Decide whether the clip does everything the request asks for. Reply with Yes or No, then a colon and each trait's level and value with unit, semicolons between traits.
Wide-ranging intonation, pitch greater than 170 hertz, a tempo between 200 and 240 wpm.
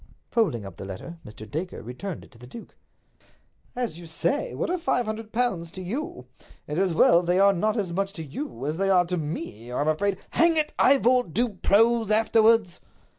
Yes: wide, 6.2 semitones; high, 190 Hz; fast, 205 wpm